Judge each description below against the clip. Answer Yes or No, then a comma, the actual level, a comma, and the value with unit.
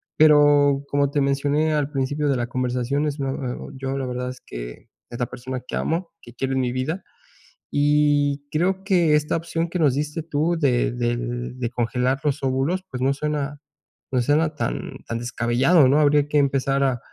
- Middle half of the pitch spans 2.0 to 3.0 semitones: Yes, average, 2.7 semitones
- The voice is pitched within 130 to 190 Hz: Yes, medium, 140 Hz